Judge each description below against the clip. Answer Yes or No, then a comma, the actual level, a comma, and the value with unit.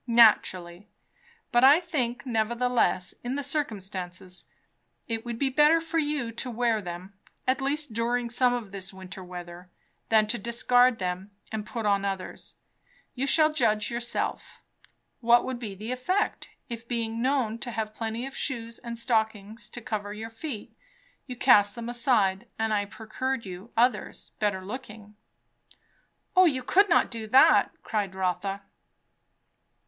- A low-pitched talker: No, high, 230 Hz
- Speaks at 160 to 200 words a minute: No, average, 150 wpm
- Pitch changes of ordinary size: Yes, average, 3.6 semitones